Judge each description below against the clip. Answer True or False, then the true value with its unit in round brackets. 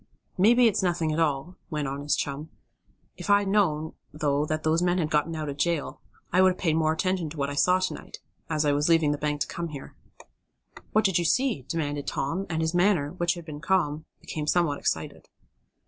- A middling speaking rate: False (225 wpm)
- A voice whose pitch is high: False (160 Hz)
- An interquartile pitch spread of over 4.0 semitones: False (3.4 semitones)